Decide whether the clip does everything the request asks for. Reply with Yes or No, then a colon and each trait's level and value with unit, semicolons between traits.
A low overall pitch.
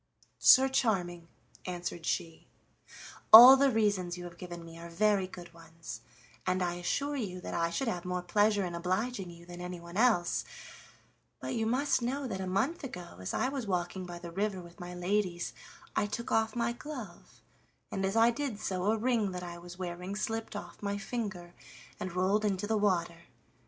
No: medium, 185 Hz